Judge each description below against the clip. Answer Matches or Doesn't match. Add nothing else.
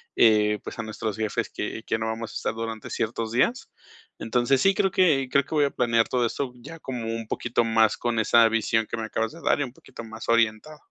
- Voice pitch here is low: Matches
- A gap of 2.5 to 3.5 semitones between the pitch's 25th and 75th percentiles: Matches